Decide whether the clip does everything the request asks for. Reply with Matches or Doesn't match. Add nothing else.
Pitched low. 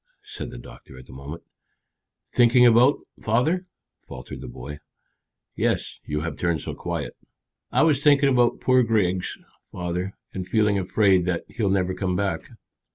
Matches